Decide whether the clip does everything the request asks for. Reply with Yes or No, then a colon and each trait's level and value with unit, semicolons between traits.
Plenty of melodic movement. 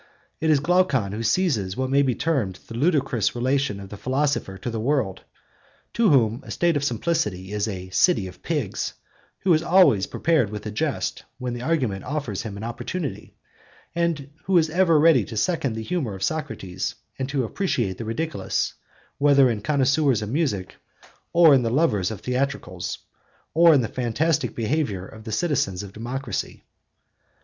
Yes: wide, 6.6 semitones